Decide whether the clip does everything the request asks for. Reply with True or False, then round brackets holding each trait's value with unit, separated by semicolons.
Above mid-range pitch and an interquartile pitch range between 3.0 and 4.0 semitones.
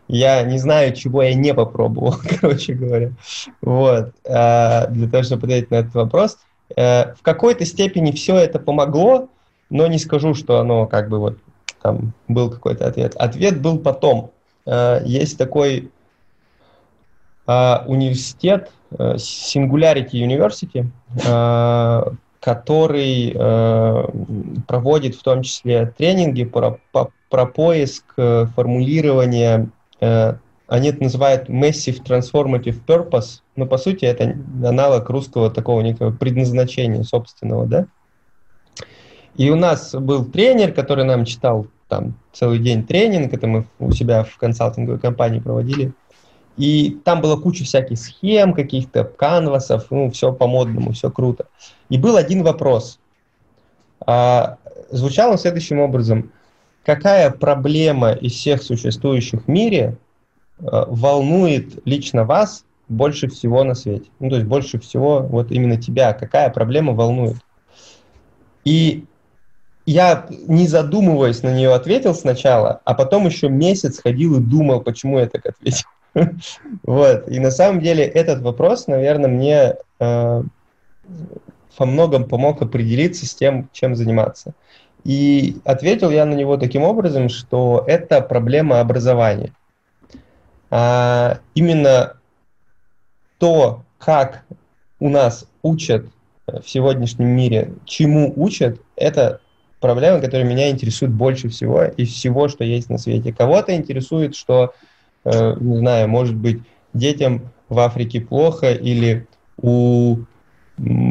False (130 Hz; 3.7 semitones)